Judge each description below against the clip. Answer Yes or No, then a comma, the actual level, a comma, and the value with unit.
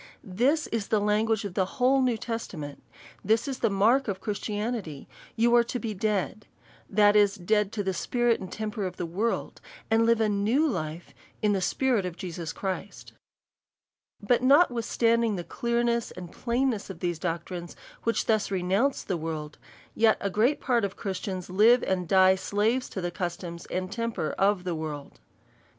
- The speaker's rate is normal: Yes, average, 170 wpm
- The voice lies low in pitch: No, high, 205 Hz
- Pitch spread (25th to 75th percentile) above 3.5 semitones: Yes, average, 4.0 semitones